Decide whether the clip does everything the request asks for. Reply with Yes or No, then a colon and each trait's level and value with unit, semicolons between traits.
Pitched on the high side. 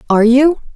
Yes: very high, 260 Hz